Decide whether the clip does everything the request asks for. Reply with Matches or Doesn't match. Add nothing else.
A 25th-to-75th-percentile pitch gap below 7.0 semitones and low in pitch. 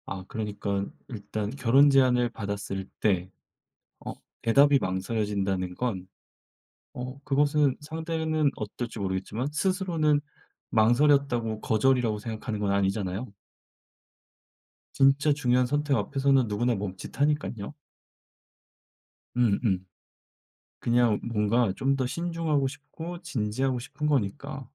Matches